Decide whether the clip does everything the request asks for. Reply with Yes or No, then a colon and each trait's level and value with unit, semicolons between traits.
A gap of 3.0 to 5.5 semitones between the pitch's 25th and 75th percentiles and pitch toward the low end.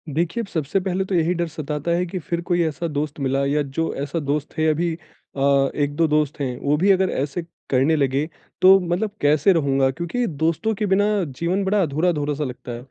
No: average, 3.7 semitones; medium, 160 Hz